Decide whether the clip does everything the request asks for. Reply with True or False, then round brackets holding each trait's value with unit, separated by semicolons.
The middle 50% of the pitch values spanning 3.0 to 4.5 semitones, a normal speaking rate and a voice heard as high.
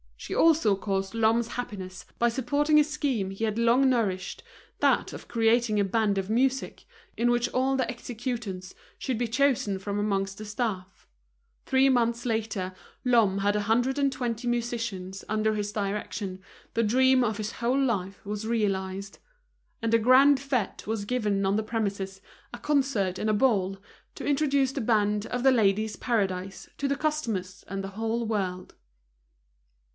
True (3.8 semitones; 165 wpm; 225 Hz)